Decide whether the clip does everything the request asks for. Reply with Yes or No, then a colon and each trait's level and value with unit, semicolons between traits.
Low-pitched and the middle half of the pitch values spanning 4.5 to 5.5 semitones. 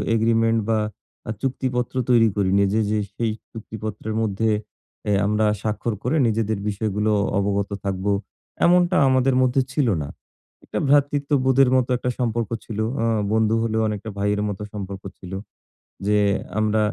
No: low, 110 Hz; average, 3.2 semitones